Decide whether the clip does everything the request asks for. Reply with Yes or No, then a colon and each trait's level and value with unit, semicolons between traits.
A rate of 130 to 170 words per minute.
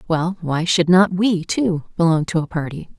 No: average, 200 wpm